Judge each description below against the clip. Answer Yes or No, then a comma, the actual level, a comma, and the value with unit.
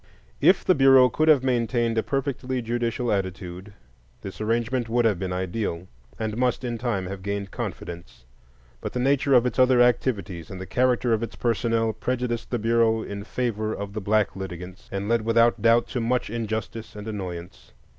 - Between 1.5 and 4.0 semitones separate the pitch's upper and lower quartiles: Yes, average, 3.5 semitones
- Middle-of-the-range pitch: No, low, 115 Hz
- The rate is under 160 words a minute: No, average, 180 wpm